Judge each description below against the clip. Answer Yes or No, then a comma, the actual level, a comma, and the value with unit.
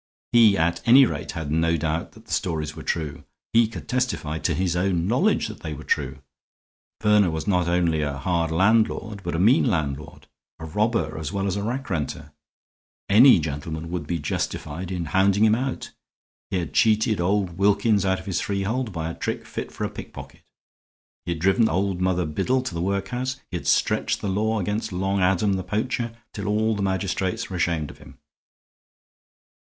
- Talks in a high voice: No, very low, 95 Hz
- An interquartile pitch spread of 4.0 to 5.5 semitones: Yes, average, 4.5 semitones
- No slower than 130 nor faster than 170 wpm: No, average, 190 wpm